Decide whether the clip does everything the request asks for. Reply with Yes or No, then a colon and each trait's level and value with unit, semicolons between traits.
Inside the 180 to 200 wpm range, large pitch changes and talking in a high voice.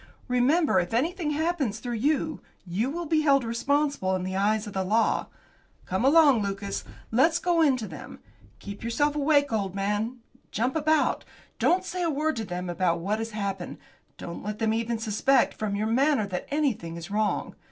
Yes: average, 185 wpm; wide, 6.6 semitones; high, 230 Hz